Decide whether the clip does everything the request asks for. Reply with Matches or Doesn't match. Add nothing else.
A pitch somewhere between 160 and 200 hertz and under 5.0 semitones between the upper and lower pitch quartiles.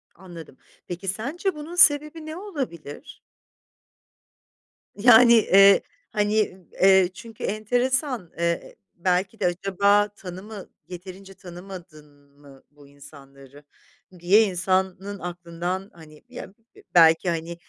Matches